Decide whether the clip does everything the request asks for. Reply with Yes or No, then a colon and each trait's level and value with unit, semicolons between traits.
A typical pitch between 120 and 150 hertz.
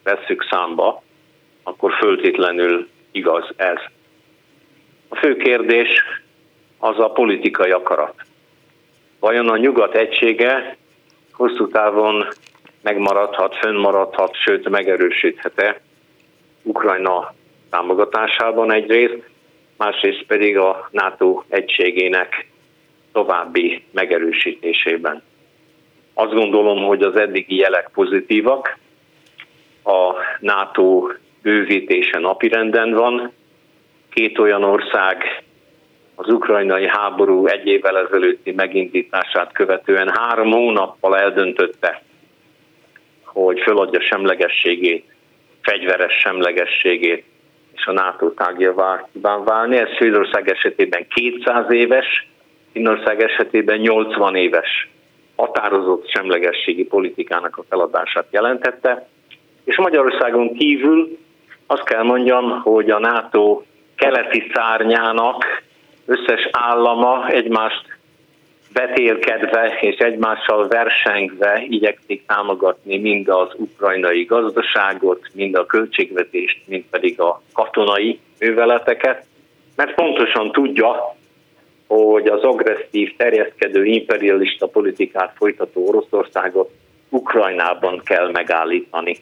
Yes: low, 125 Hz